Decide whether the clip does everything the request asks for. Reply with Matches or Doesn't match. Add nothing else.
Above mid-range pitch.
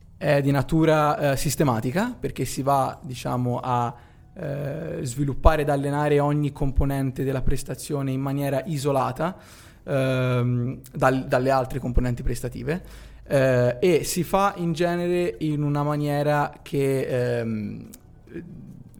Doesn't match